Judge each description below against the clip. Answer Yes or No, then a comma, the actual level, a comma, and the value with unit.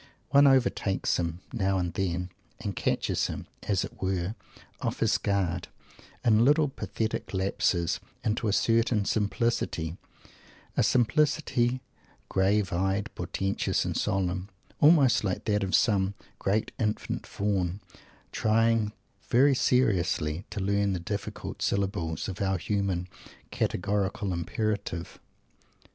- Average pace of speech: No, slow, 120 wpm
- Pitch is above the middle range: No, low, 100 Hz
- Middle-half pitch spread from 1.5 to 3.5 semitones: Yes, average, 3.2 semitones